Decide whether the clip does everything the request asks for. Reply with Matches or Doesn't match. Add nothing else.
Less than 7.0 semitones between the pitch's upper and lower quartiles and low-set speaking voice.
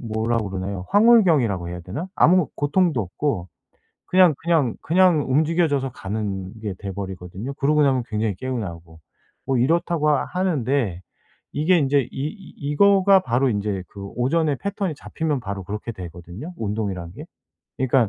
Doesn't match